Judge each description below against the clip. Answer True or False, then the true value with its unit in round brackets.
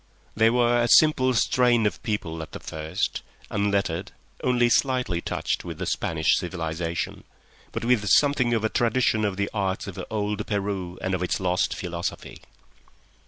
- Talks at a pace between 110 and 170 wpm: True (160 wpm)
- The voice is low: True (105 Hz)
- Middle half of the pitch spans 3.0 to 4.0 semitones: False (4.8 semitones)